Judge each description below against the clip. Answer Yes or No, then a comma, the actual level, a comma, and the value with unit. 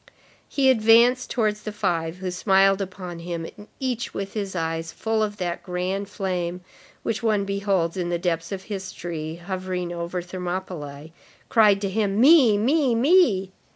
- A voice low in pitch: No, high, 190 Hz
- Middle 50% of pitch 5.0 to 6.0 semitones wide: No, average, 3.6 semitones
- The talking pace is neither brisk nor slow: Yes, average, 155 wpm